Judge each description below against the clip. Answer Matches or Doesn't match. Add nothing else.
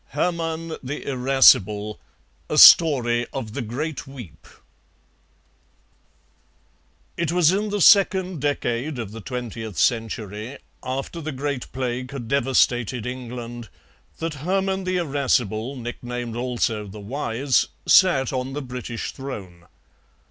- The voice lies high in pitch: Doesn't match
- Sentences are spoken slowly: Matches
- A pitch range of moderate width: Matches